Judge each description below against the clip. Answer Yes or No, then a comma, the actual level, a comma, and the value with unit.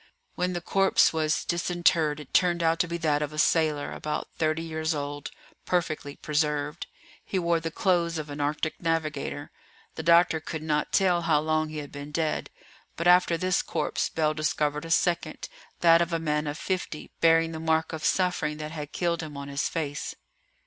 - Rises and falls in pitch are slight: Yes, narrow, 2.0 semitones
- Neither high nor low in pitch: Yes, medium, 160 Hz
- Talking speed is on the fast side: No, average, 190 wpm